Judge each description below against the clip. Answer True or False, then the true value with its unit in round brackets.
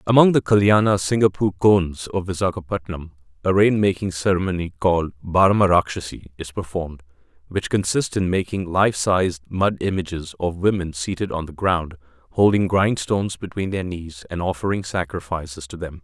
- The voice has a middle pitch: False (90 Hz)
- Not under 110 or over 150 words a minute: True (140 wpm)